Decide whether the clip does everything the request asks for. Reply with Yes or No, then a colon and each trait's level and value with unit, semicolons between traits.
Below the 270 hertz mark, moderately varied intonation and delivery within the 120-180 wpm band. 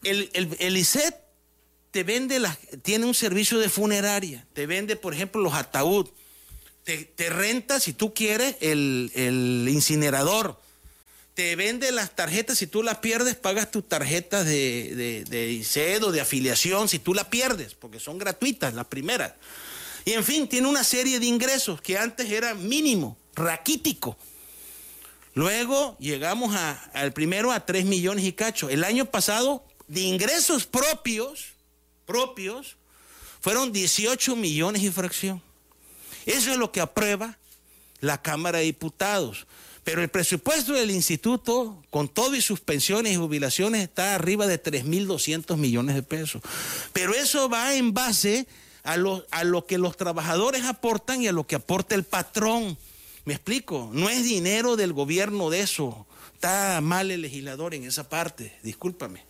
No: high, 190 Hz; wide, 7.1 semitones; average, 155 wpm